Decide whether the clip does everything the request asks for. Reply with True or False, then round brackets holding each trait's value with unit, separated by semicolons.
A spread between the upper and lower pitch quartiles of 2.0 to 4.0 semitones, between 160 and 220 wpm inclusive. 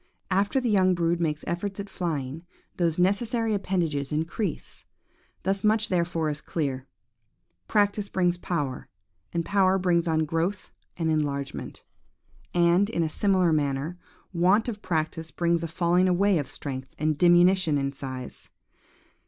False (3.6 semitones; 140 wpm)